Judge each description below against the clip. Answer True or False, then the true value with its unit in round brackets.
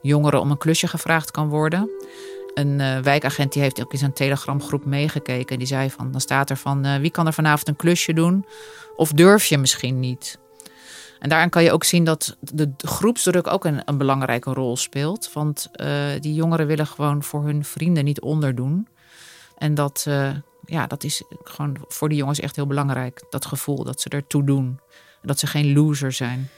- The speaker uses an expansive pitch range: False (2.7 semitones)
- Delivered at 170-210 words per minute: True (200 wpm)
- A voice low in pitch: False (145 Hz)